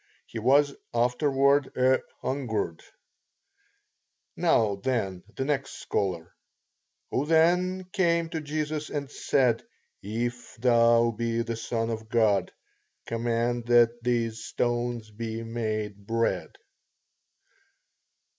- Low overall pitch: Yes, low, 120 Hz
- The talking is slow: Yes, slow, 100 wpm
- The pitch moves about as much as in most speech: Yes, average, 3.3 semitones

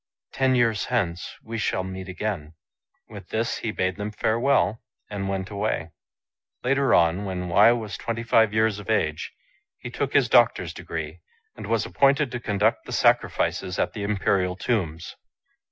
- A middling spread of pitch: Yes, average, 3.9 semitones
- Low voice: Yes, low, 105 Hz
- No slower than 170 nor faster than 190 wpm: No, average, 160 wpm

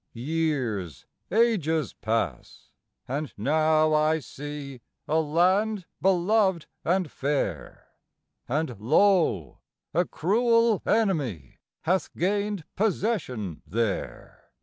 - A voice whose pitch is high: No, medium, 155 Hz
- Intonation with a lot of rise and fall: Yes, wide, 7.1 semitones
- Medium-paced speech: No, slow, 85 wpm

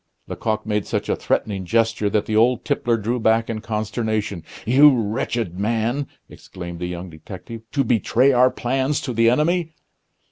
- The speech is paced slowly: No, average, 165 wpm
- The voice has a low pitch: Yes, low, 115 Hz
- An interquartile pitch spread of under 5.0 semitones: Yes, average, 3.1 semitones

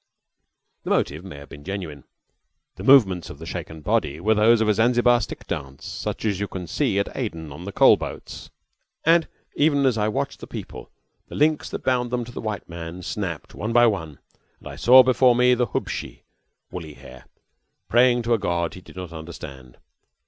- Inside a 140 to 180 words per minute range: No, average, 195 wpm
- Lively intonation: Yes, wide, 6.7 semitones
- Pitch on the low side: Yes, low, 100 Hz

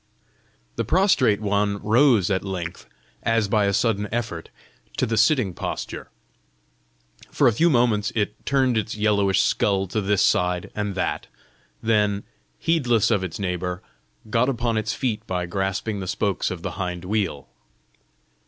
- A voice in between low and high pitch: No, low, 105 Hz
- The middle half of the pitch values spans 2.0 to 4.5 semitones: Yes, average, 3.1 semitones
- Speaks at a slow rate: No, average, 150 wpm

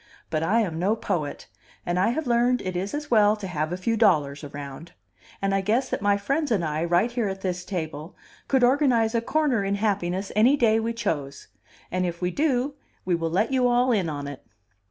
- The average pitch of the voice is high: Yes, high, 200 Hz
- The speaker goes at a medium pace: No, fast, 215 wpm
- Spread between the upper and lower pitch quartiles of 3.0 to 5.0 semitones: No, wide, 5.5 semitones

